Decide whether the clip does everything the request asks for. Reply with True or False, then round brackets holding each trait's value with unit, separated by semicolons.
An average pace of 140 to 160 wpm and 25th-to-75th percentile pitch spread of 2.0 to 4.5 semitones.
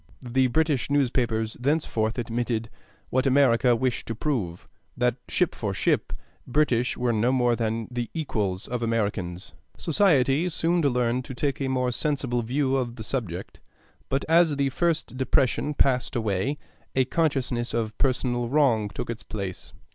True (150 wpm; 3.3 semitones)